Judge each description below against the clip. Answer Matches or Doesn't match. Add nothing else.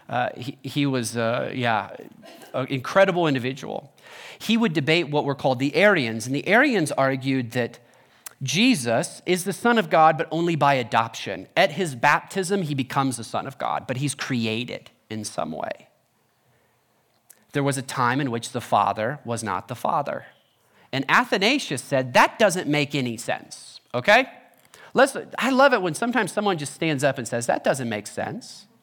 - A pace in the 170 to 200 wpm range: Matches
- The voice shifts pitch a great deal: Matches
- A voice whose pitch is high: Doesn't match